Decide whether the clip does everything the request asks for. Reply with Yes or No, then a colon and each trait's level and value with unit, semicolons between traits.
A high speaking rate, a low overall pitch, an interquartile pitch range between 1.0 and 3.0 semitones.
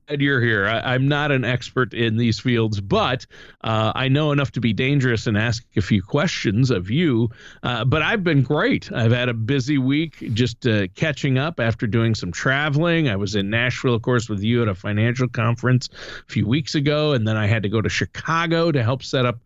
No: fast, 220 wpm; low, 125 Hz; average, 3.8 semitones